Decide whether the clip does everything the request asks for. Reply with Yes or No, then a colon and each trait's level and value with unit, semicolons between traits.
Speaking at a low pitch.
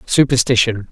Yes: low, 120 Hz